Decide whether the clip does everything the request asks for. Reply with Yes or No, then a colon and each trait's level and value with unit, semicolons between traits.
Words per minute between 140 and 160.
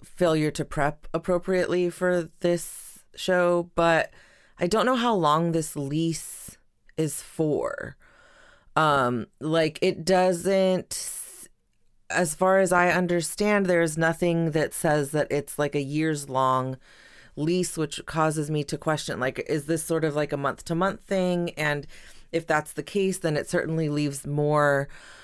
Yes: average, 150 wpm